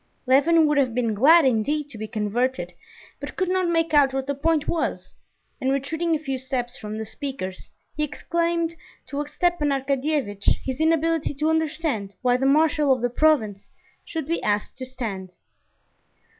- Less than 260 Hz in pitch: No, very high, 280 Hz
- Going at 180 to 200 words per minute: No, average, 170 wpm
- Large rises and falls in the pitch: No, average, 4.4 semitones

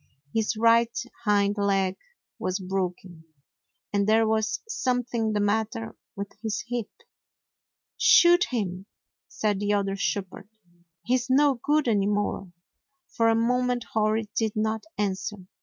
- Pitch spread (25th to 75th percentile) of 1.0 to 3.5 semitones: Yes, narrow, 2.6 semitones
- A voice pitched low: No, high, 215 Hz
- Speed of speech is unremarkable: No, slow, 125 wpm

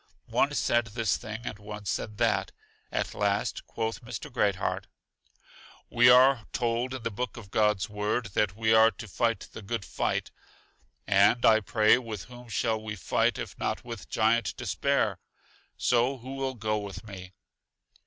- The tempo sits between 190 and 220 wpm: No, average, 165 wpm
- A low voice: Yes, low, 110 Hz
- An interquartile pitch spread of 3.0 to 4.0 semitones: No, narrow, 2.4 semitones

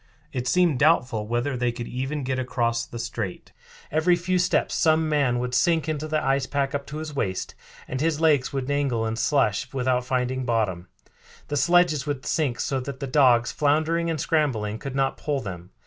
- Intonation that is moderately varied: Yes, average, 3.9 semitones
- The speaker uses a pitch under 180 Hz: Yes, low, 135 Hz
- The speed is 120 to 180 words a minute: No, average, 195 wpm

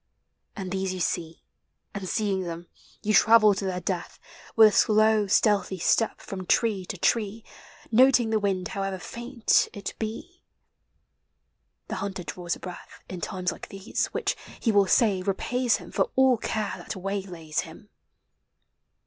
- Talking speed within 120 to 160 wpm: Yes, average, 155 wpm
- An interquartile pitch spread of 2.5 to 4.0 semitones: Yes, average, 2.9 semitones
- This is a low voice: No, high, 200 Hz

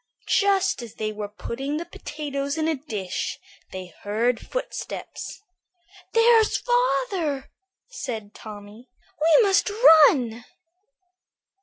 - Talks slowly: Yes, slow, 105 wpm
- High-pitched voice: Yes, very high, 280 Hz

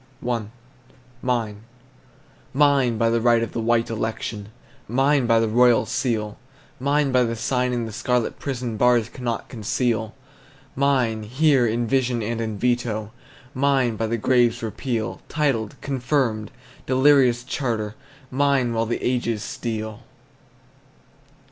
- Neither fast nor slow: No, slow, 130 wpm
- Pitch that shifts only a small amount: Yes, narrow, 2.3 semitones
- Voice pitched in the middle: No, low, 120 Hz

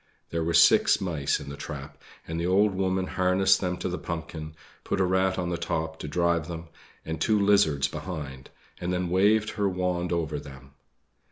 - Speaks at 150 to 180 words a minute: No, average, 190 wpm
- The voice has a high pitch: No, very low, 85 Hz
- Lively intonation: No, average, 2.9 semitones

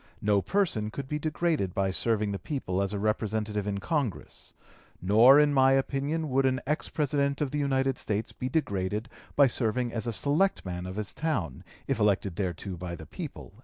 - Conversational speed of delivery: Yes, average, 185 wpm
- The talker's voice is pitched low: Yes, low, 115 Hz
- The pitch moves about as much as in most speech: No, wide, 6.0 semitones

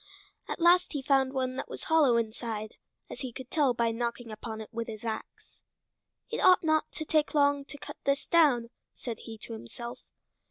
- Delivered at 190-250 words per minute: Yes, average, 195 wpm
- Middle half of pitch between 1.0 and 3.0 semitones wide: No, average, 4.0 semitones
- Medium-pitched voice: No, very high, 255 Hz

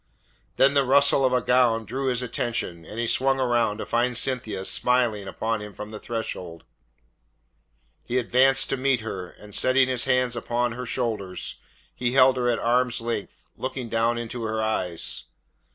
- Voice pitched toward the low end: Yes, low, 120 Hz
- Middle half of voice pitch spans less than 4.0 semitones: Yes, narrow, 2.5 semitones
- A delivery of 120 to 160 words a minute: No, average, 170 wpm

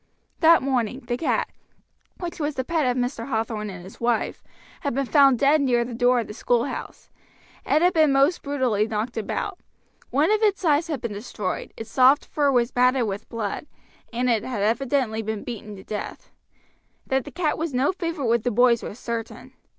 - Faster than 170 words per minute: Yes, average, 195 wpm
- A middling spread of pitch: Yes, average, 4.1 semitones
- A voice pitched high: Yes, very high, 250 Hz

